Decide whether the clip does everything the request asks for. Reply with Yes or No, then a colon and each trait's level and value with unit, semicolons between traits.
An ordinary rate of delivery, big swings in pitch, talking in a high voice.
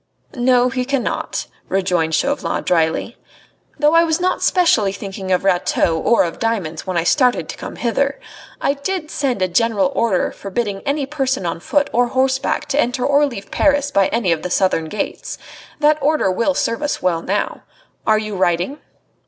Yes: average, 175 wpm; wide, 7.0 semitones; high, 235 Hz